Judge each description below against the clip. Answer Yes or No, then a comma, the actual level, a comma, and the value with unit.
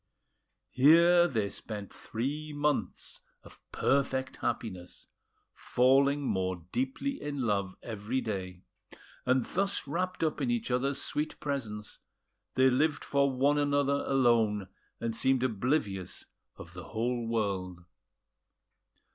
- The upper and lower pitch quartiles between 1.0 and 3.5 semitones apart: No, average, 5.2 semitones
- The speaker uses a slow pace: Yes, slow, 115 wpm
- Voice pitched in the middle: No, low, 130 Hz